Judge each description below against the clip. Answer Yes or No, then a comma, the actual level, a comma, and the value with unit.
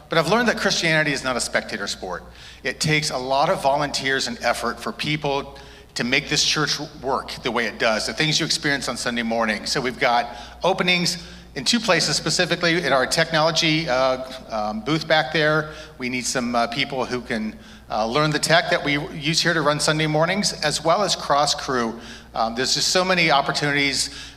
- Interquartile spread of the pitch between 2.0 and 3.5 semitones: No, average, 3.9 semitones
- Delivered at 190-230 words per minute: Yes, average, 200 wpm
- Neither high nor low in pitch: Yes, medium, 145 Hz